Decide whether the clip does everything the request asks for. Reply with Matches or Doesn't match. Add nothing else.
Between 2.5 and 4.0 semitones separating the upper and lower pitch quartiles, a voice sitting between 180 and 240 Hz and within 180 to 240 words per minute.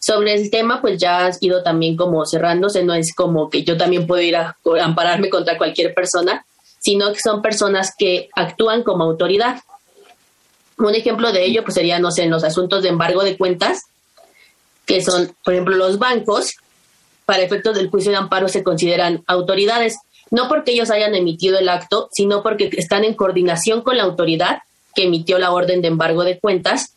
Matches